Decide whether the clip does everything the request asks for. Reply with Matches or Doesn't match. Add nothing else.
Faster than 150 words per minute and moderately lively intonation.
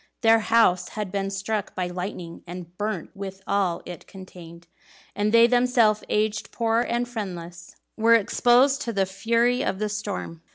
Matches